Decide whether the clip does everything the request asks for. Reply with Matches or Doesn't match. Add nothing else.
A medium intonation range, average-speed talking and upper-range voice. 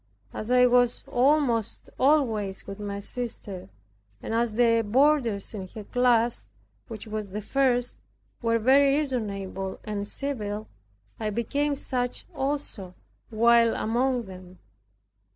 Doesn't match